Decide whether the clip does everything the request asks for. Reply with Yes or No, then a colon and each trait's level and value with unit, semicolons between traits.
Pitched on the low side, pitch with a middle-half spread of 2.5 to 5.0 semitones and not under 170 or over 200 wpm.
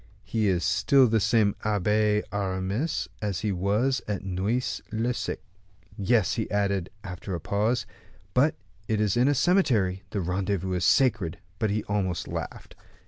No: low, 105 Hz; average, 3.2 semitones; average, 160 wpm